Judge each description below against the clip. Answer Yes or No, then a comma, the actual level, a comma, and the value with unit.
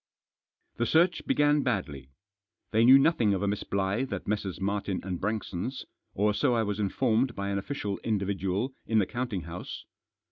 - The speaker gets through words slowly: No, average, 170 wpm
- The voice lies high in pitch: No, low, 105 Hz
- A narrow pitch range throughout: No, average, 3.9 semitones